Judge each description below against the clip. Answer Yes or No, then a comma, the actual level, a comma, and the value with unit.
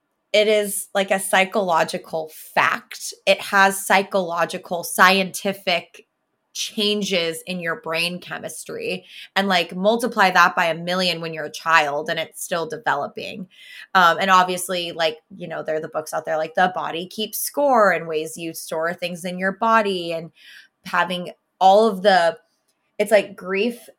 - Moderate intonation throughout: Yes, average, 3.3 semitones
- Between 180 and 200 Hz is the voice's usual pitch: Yes, medium, 185 Hz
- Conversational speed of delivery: Yes, average, 155 wpm